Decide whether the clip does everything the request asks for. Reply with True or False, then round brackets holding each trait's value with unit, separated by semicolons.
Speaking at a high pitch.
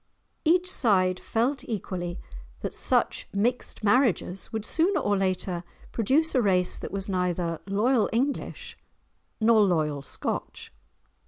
True (205 Hz)